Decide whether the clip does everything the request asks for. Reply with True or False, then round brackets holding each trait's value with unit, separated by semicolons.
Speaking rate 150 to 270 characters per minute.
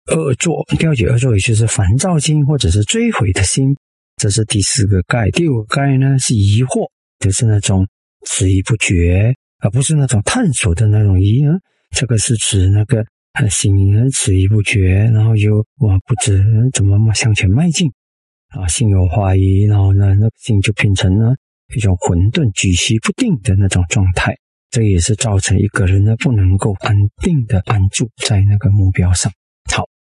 True (255 characters per minute)